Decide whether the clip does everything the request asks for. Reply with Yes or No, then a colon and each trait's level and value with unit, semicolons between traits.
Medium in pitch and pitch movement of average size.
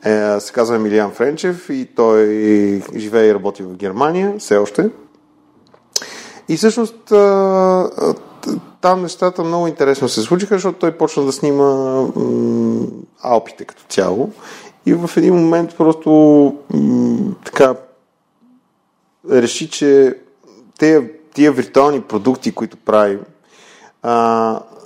No: medium, 145 Hz; wide, 8.1 semitones